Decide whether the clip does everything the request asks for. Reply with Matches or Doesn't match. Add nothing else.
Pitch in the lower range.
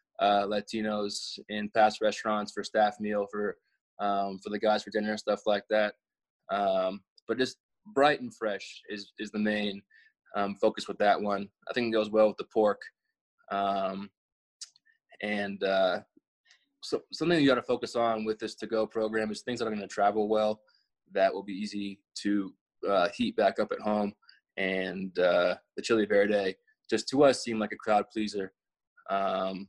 Matches